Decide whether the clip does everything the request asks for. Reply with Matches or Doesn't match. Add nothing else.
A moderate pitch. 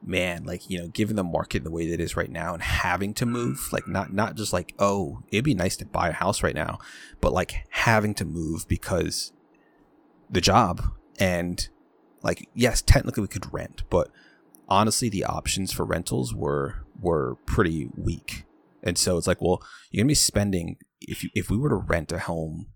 Doesn't match